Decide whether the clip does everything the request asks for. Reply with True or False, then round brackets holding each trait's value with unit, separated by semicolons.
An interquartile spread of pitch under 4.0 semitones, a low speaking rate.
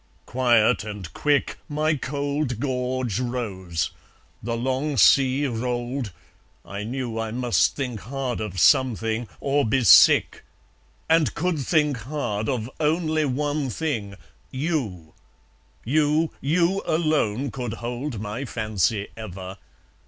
False (4.7 semitones; 115 wpm)